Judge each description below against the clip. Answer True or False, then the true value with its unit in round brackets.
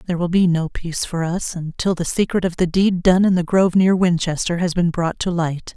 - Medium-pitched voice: True (175 Hz)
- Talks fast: True (250 wpm)